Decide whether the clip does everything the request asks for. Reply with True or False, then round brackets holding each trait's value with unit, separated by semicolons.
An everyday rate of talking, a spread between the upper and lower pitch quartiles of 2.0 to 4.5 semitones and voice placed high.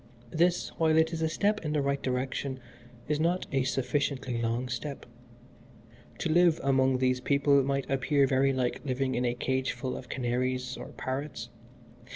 False (165 wpm; 2.7 semitones; 135 Hz)